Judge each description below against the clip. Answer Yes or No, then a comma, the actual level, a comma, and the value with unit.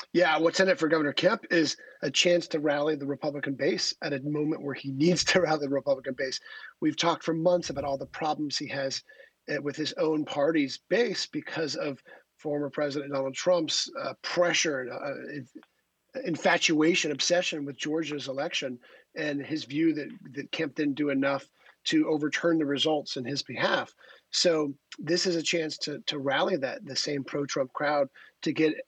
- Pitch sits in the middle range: Yes, medium, 150 Hz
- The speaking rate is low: No, average, 180 wpm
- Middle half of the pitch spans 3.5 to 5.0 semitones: No, narrow, 2.6 semitones